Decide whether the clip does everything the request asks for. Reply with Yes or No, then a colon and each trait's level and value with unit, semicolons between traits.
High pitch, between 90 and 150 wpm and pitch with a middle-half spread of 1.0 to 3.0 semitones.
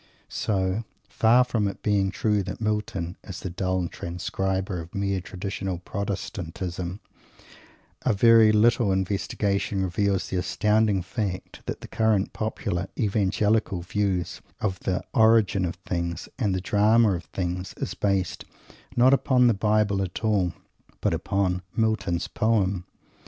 No: low, 100 Hz; slow, 135 wpm; narrow, 2.6 semitones